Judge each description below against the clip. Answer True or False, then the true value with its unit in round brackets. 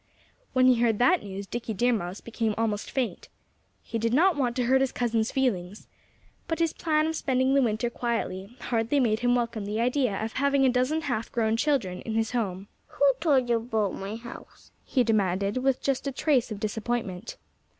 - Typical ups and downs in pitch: True (3.4 semitones)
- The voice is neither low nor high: False (235 Hz)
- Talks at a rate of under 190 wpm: False (195 wpm)